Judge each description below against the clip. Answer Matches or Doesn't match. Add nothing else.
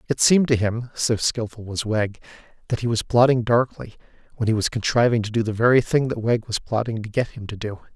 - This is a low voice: Matches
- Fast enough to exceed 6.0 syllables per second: Doesn't match